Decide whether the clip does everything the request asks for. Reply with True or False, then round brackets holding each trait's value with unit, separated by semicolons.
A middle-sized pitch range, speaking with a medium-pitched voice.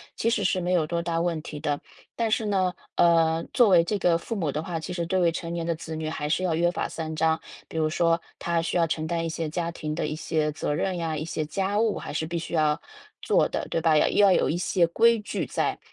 False (2.2 semitones; 165 Hz)